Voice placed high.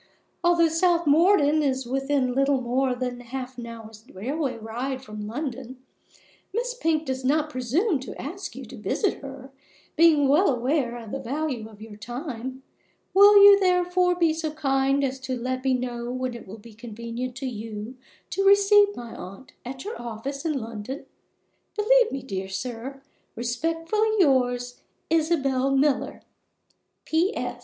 Yes: very high, 265 Hz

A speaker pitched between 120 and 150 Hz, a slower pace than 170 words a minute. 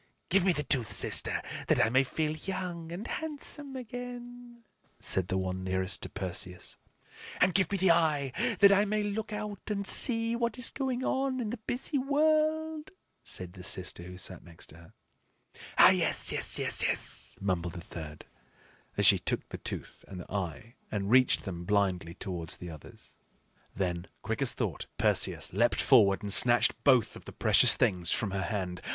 No: low, 135 Hz; average, 180 wpm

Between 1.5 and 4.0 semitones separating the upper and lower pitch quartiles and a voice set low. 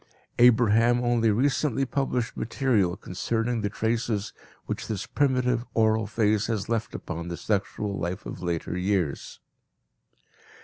Yes: average, 3.2 semitones; low, 110 Hz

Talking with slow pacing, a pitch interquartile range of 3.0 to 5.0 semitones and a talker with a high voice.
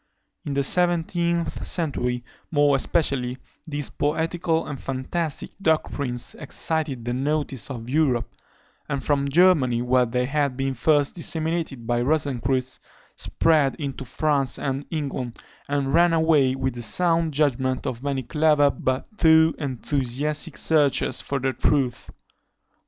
No: slow, 130 wpm; average, 3.5 semitones; medium, 140 Hz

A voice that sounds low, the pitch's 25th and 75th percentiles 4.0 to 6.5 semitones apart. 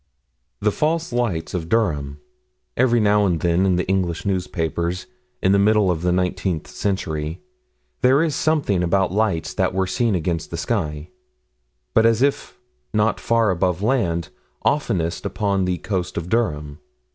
Yes: very low, 95 Hz; average, 4.5 semitones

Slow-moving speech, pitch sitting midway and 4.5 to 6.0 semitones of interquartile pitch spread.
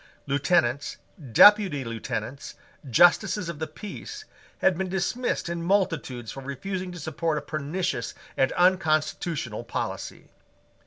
Yes: slow, 115 wpm; medium, 165 Hz; average, 5.2 semitones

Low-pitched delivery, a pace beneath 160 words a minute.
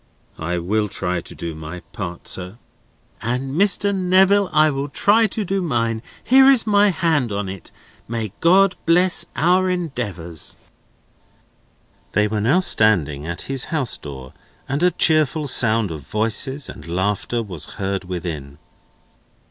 Yes: low, 115 Hz; average, 145 wpm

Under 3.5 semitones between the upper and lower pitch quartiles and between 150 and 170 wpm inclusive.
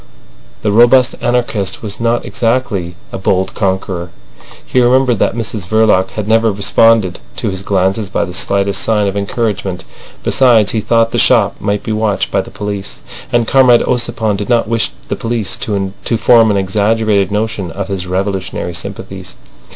Yes: average, 2.9 semitones; average, 165 wpm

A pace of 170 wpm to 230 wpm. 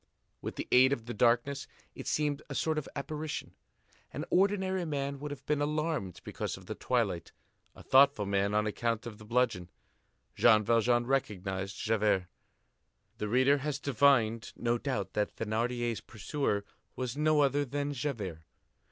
No: average, 155 wpm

